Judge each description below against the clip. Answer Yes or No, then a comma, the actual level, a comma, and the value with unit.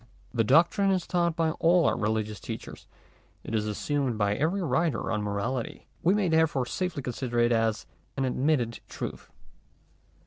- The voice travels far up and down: Yes, wide, 6.5 semitones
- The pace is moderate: Yes, average, 160 wpm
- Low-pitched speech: Yes, low, 130 Hz